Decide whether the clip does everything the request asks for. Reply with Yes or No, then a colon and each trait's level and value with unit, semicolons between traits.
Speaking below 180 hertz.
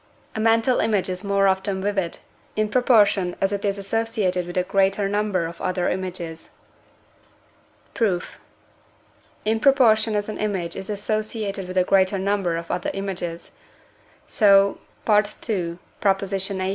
No: high, 195 Hz